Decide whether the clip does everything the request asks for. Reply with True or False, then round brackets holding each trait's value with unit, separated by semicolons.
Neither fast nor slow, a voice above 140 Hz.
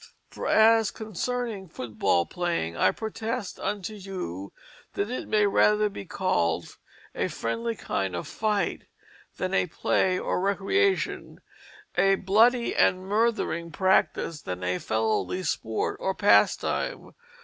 False (125 wpm; 190 Hz)